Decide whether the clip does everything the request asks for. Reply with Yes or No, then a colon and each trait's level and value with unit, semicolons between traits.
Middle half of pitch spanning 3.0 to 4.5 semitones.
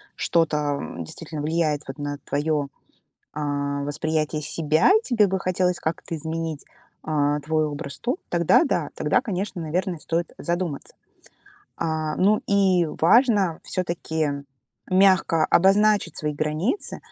Yes: average, 3.4 semitones